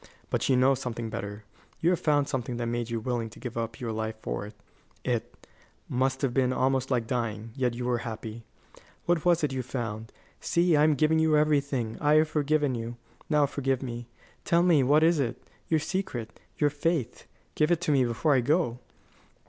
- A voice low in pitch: Yes, low, 130 Hz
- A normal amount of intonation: Yes, average, 4.4 semitones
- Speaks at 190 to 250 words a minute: Yes, average, 195 wpm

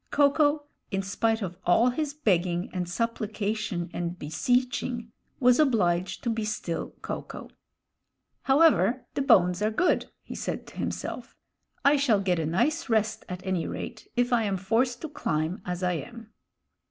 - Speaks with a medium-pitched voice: No, high, 220 Hz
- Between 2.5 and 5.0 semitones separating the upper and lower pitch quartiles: No, wide, 5.6 semitones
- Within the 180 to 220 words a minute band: No, average, 165 wpm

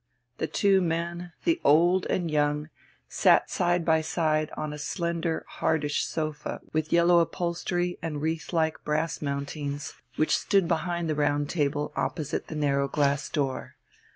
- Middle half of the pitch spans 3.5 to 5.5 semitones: No, narrow, 2.5 semitones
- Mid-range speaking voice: Yes, medium, 160 Hz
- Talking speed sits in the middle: Yes, average, 150 wpm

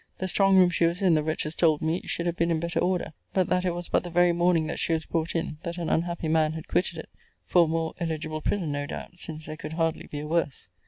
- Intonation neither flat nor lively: No, narrow, 1.9 semitones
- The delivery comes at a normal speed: No, fast, 275 wpm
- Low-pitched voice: No, medium, 165 Hz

